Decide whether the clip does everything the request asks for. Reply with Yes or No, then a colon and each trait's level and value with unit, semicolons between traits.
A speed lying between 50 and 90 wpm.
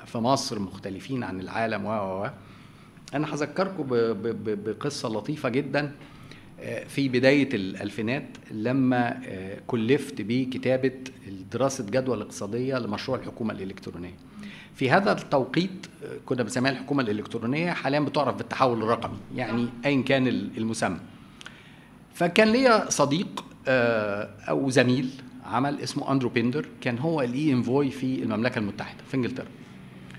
No: average, 110 wpm